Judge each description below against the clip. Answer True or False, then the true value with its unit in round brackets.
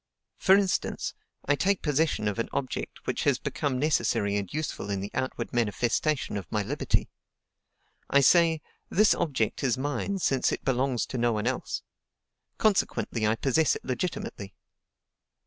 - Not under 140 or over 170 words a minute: True (150 wpm)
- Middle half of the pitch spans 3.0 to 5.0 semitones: False (5.6 semitones)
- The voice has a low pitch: True (130 Hz)